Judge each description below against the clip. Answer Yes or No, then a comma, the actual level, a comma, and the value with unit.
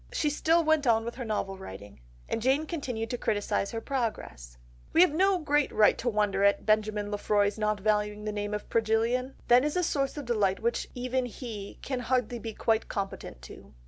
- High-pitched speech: Yes, high, 225 Hz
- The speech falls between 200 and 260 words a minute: Yes, fast, 205 wpm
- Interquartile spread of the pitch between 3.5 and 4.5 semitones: Yes, average, 4.0 semitones